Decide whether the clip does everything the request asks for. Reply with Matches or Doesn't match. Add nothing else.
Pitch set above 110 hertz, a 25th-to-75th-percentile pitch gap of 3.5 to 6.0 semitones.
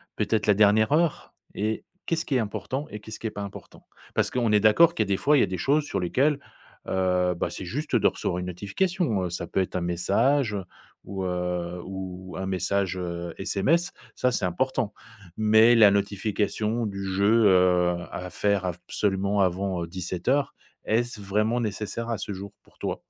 Doesn't match